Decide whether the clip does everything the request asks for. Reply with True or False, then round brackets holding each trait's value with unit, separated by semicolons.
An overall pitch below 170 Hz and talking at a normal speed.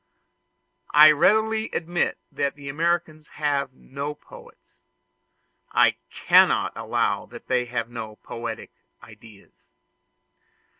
False (140 Hz; 100 wpm)